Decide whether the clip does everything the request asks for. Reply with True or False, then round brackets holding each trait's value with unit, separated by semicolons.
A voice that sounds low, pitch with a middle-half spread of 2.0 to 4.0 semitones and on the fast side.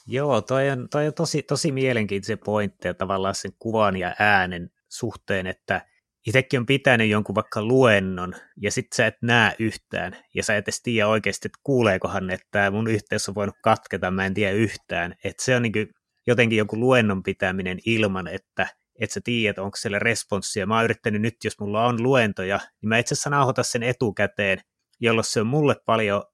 True (110 Hz; 3.7 semitones; 190 wpm)